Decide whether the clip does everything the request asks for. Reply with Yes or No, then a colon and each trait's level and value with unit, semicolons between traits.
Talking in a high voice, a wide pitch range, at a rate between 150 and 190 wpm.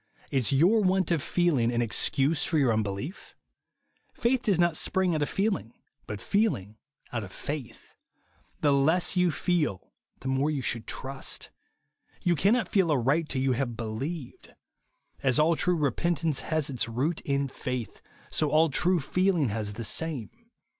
No: medium, 145 Hz; wide, 5.8 semitones; average, 160 wpm